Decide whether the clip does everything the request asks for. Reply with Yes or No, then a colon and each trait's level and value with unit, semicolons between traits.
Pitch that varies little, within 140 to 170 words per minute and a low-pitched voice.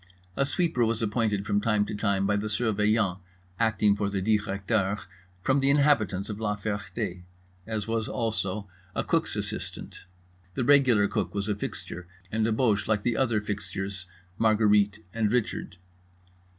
Yes: narrow, 2.0 semitones; average, 155 wpm; low, 105 Hz